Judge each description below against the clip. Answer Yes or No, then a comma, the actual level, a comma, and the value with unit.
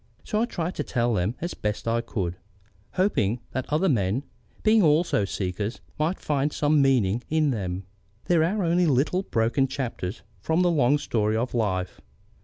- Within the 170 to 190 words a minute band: Yes, average, 175 wpm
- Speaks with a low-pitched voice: Yes, low, 130 Hz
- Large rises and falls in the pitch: Yes, wide, 7.1 semitones